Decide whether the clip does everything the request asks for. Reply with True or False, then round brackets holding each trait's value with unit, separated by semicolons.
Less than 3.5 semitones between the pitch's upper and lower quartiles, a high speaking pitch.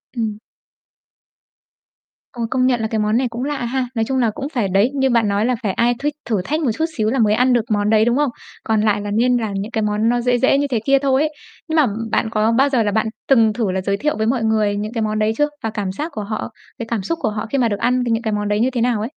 True (3.1 semitones; 230 Hz)